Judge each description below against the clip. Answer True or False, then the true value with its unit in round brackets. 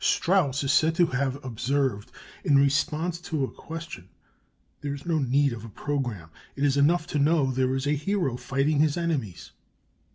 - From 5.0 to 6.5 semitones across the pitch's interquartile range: False (3.1 semitones)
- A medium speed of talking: True (175 wpm)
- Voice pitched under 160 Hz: True (140 Hz)